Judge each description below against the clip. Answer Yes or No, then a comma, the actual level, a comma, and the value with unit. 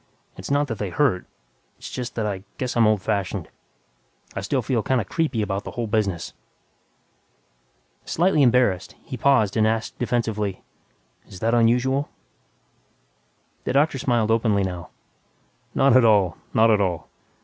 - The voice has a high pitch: No, low, 115 Hz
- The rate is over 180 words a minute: No, average, 150 wpm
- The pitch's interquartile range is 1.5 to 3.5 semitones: No, average, 3.9 semitones